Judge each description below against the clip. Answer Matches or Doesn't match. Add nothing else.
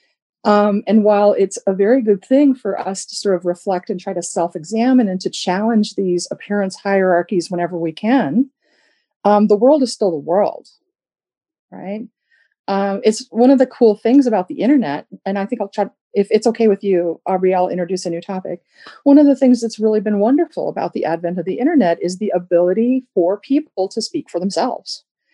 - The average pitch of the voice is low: Doesn't match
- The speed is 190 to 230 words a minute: Matches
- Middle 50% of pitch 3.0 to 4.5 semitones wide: Doesn't match